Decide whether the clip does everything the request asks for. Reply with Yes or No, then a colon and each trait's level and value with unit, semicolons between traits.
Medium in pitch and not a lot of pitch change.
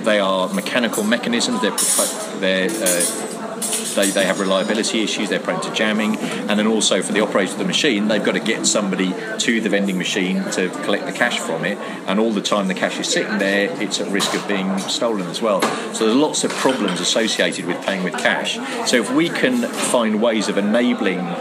No: low, 100 Hz; narrow, 2.0 semitones